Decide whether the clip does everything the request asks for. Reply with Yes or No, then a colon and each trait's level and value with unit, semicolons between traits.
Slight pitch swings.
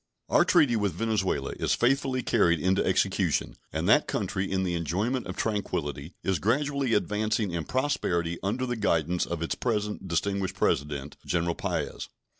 No: average, 5.0 semitones